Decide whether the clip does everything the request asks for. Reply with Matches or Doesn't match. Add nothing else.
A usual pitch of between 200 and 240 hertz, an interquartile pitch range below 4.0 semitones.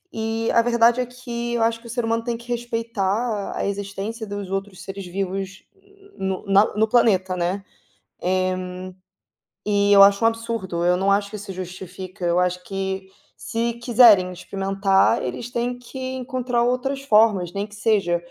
Matches